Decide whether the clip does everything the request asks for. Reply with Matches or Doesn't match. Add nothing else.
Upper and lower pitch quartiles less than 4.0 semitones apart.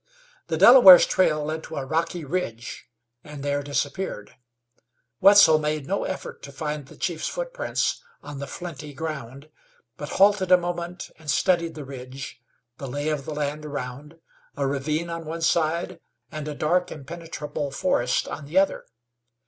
Matches